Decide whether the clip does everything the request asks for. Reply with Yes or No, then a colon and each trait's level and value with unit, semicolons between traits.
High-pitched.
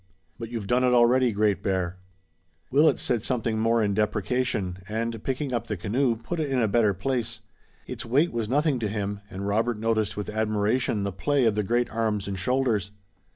No: low, 115 Hz